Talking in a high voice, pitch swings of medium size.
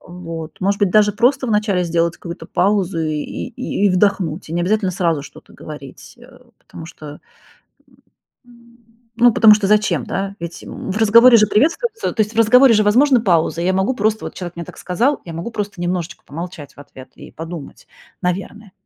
Yes: high, 195 Hz; average, 4.3 semitones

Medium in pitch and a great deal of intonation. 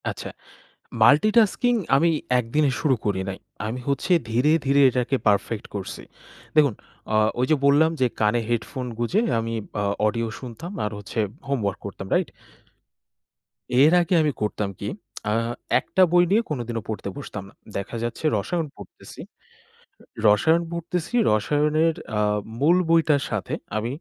No: low, 130 Hz; wide, 6.6 semitones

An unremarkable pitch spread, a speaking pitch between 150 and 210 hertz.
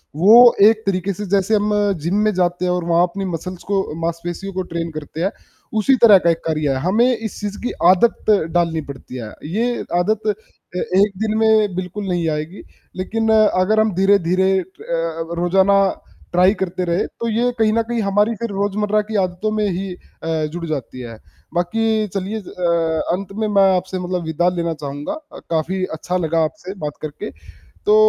Yes: average, 3.6 semitones; high, 190 Hz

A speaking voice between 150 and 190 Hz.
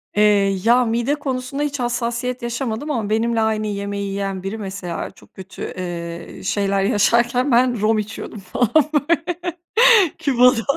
No: high, 225 Hz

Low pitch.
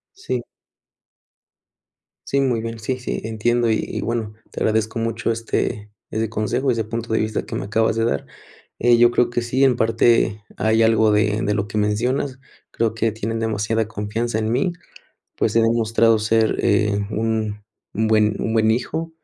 Yes: low, 115 Hz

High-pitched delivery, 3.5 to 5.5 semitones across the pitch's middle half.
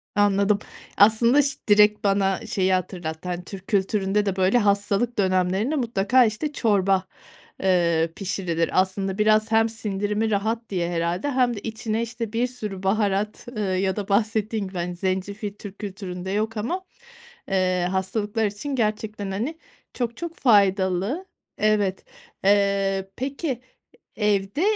No: high, 205 Hz; average, 2.7 semitones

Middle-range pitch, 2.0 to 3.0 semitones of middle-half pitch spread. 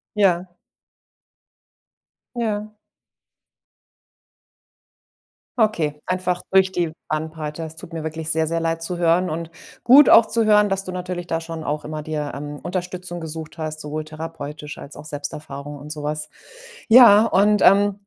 No: medium, 165 Hz; average, 3.4 semitones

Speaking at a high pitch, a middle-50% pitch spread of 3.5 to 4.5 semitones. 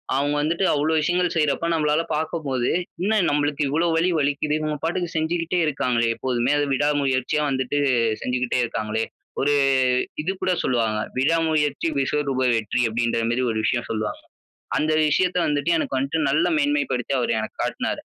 No: medium, 145 Hz; average, 3.9 semitones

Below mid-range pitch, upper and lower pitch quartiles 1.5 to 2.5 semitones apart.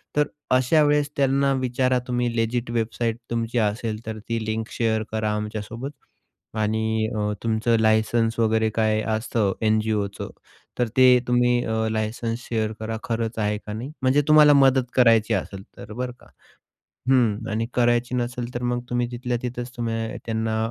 Yes: low, 115 Hz; narrow, 1.9 semitones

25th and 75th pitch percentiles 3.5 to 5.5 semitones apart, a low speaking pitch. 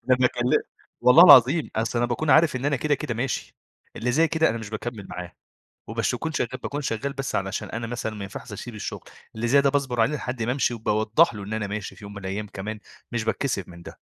Yes: average, 4.0 semitones; low, 120 Hz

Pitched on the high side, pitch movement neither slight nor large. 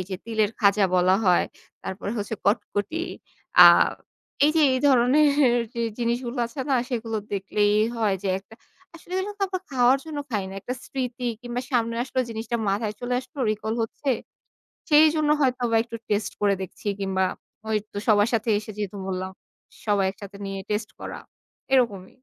Yes: high, 225 Hz; average, 4.0 semitones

